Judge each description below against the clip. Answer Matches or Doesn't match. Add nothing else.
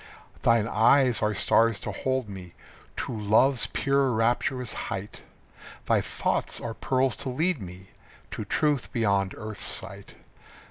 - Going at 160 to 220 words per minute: Doesn't match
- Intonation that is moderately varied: Matches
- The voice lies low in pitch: Matches